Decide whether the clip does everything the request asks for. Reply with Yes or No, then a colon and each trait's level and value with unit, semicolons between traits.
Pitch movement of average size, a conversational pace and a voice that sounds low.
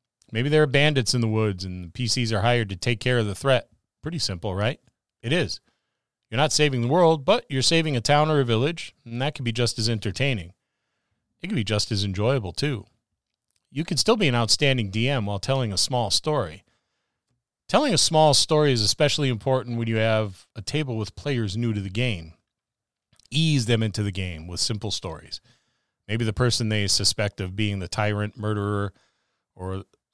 Yes: average, 4.2 semitones; average, 195 wpm; low, 115 Hz